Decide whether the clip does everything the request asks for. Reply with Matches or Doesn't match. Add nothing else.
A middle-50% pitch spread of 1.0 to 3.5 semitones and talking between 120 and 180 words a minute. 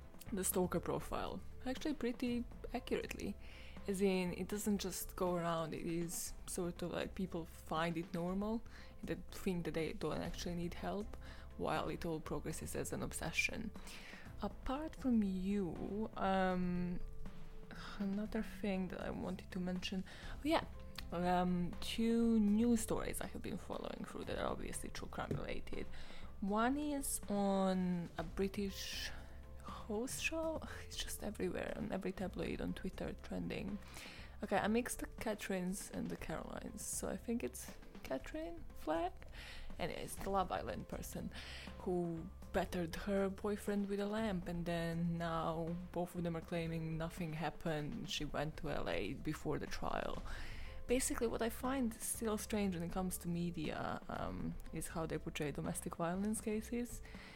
Doesn't match